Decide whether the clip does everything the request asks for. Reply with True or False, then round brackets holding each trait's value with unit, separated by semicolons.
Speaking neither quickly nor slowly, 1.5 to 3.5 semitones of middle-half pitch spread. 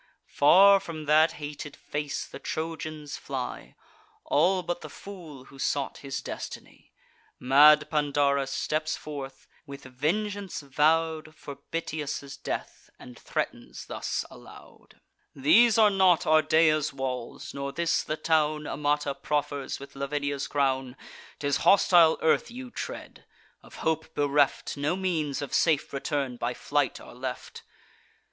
False (130 wpm; 2.4 semitones)